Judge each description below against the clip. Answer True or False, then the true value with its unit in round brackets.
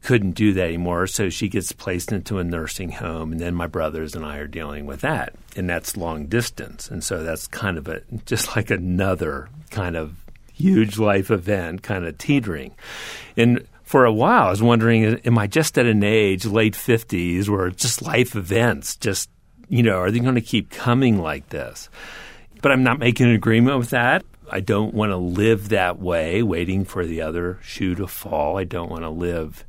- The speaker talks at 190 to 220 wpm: True (200 wpm)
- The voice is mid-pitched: False (100 Hz)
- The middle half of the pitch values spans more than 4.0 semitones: True (4.7 semitones)